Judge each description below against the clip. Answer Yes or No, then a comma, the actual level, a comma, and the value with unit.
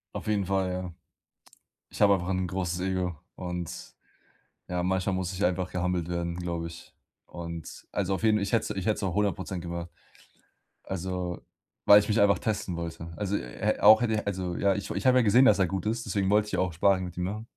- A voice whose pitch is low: Yes, very low, 95 Hz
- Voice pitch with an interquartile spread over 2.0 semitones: Yes, narrow, 2.5 semitones